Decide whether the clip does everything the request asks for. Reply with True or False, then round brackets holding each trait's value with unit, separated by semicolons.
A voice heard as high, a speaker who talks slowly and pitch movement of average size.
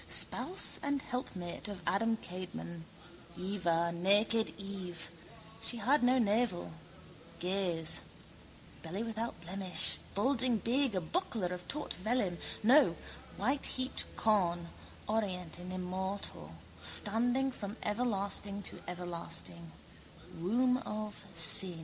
True (200 Hz; 95 wpm; 4.6 semitones)